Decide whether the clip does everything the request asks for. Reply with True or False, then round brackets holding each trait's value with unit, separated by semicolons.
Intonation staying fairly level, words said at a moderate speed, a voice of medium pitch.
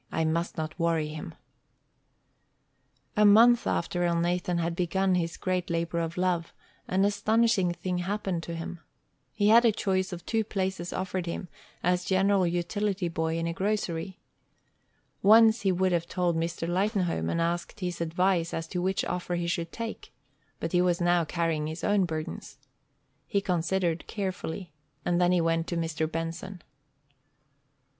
True (2.3 semitones; 160 wpm; 175 Hz)